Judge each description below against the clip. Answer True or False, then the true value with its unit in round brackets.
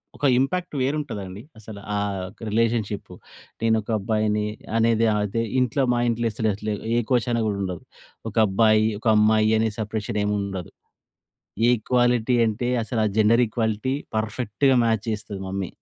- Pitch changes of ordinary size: False (2.0 semitones)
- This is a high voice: False (110 Hz)